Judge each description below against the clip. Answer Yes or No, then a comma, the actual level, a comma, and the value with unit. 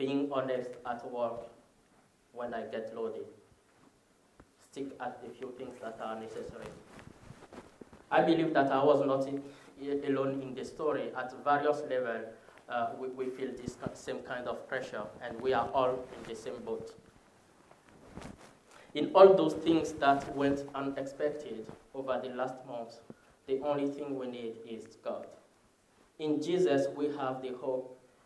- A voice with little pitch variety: Yes, narrow, 2.2 semitones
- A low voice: Yes, low, 130 Hz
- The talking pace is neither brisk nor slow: Yes, average, 155 wpm